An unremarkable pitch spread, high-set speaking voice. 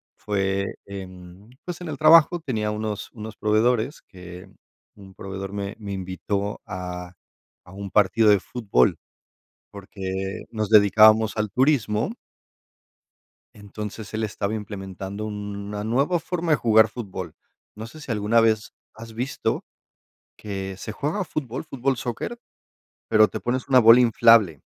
No: average, 3.0 semitones; low, 105 Hz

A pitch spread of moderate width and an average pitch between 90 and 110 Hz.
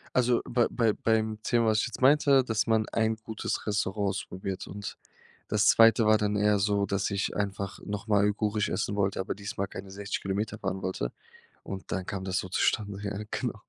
No: narrow, 1.9 semitones; low, 105 Hz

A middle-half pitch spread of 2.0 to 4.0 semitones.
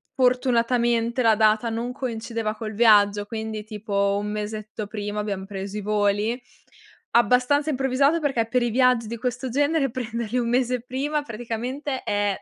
Yes: average, 2.9 semitones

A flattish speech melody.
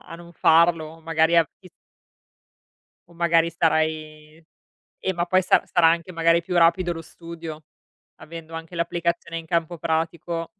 Yes: narrow, 1.0 semitones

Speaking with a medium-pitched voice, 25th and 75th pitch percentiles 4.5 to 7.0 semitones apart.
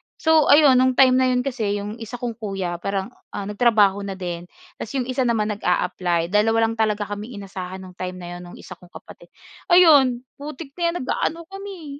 No: high, 225 Hz; average, 5.1 semitones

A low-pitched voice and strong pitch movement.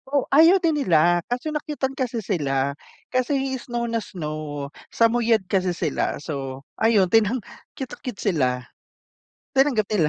No: high, 220 Hz; wide, 8.3 semitones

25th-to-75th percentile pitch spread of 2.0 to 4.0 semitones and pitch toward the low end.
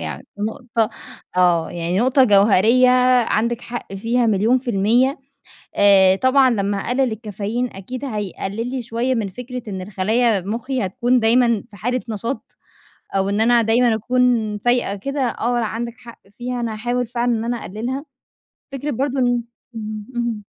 No: average, 3.2 semitones; high, 230 Hz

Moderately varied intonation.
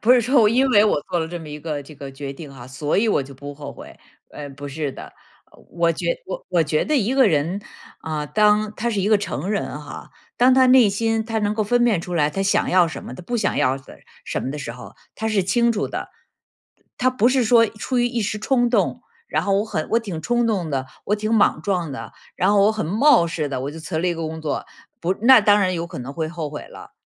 No: wide, 6.6 semitones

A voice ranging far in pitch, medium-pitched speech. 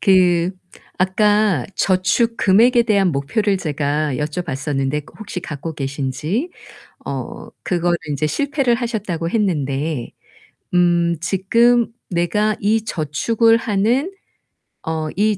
Yes: wide, 6.0 semitones; medium, 180 Hz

